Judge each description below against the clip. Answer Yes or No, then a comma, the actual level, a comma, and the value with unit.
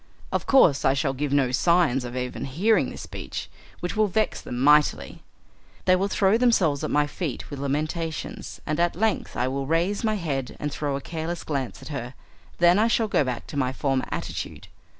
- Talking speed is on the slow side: No, average, 200 wpm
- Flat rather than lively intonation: No, average, 4.8 semitones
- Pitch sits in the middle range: Yes, medium, 150 Hz